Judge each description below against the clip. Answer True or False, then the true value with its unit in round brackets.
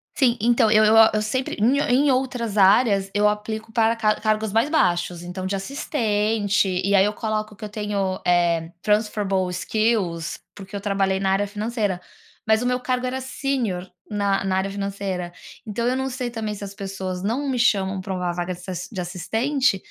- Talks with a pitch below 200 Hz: False (210 Hz)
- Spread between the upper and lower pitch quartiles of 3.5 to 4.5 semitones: False (3.1 semitones)